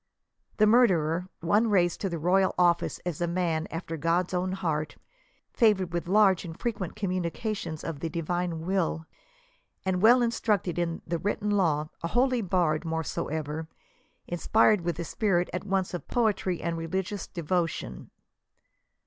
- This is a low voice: No, medium, 175 Hz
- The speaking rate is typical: Yes, average, 150 wpm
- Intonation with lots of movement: No, average, 3.0 semitones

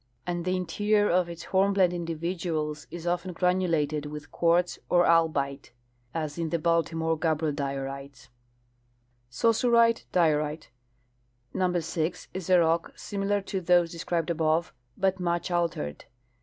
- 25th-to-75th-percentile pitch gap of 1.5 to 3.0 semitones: Yes, average, 2.7 semitones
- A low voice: No, medium, 170 Hz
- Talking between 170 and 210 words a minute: No, average, 145 wpm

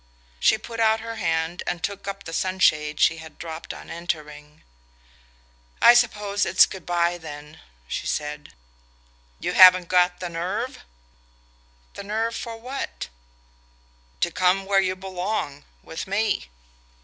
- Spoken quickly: No, slow, 135 wpm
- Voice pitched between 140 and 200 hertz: Yes, medium, 185 Hz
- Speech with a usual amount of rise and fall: Yes, average, 3.9 semitones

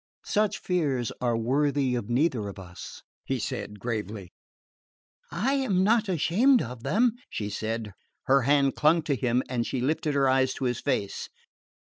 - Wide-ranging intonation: Yes, wide, 6.3 semitones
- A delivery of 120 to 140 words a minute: No, average, 155 wpm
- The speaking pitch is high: No, low, 130 Hz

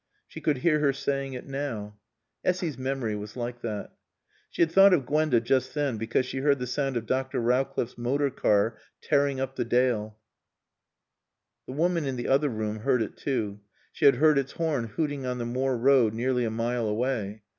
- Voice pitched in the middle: No, low, 130 Hz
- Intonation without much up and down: No, average, 3.2 semitones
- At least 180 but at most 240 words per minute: Yes, average, 190 wpm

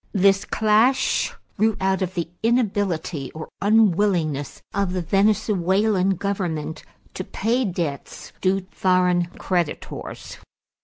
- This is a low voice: No, high, 190 Hz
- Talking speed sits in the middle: No, slow, 105 wpm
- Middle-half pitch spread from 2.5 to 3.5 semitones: Yes, average, 3.0 semitones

